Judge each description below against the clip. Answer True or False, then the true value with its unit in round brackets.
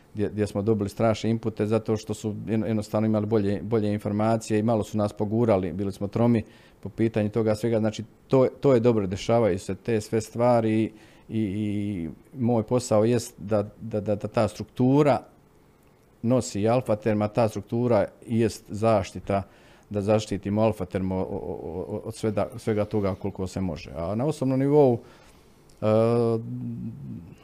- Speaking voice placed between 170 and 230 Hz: False (110 Hz)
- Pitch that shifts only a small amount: True (1.8 semitones)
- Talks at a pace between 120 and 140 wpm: False (150 wpm)